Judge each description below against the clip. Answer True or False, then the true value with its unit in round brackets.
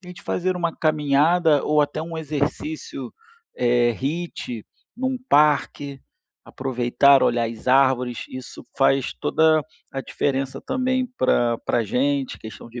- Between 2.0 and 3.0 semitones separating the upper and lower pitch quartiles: False (4.1 semitones)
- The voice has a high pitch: False (140 Hz)